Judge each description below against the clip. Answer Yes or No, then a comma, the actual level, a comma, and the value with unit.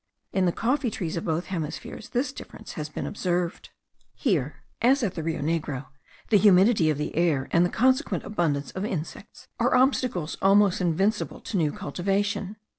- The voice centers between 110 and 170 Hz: No, medium, 180 Hz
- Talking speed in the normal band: Yes, average, 170 wpm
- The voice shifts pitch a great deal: No, average, 4.7 semitones